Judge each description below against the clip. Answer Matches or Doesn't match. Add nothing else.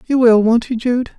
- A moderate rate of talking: Doesn't match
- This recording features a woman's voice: Doesn't match